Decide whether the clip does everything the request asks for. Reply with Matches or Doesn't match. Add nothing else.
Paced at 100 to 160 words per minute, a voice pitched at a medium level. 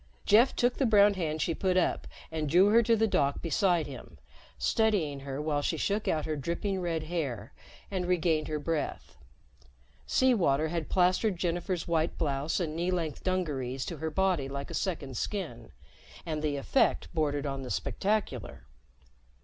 Doesn't match